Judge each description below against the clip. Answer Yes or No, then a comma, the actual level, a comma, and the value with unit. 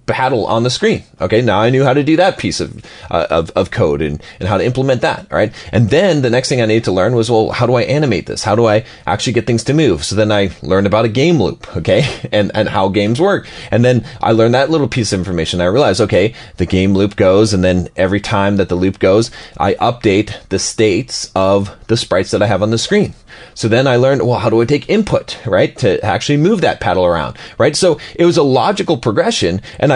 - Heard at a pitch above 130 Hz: No, low, 110 Hz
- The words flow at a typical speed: No, fast, 255 wpm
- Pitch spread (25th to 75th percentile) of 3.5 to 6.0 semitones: Yes, average, 4.3 semitones